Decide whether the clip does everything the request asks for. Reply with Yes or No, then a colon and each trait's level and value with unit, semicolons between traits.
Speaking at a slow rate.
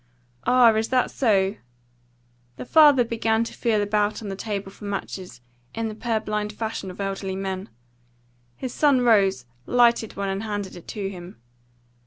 No: average, 160 wpm